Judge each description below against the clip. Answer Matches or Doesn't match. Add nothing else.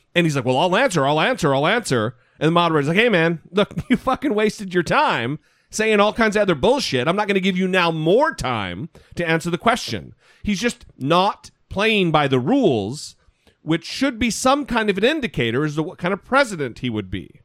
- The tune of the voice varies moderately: Doesn't match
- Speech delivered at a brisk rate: Matches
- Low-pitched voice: Doesn't match